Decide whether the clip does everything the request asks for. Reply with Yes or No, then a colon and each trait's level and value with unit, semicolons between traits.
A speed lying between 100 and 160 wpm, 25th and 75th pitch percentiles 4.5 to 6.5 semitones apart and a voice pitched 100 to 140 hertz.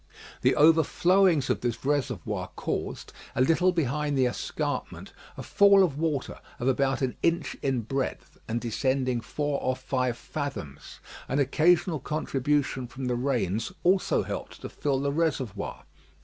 No: average, 145 wpm; average, 3.5 semitones; low, 135 Hz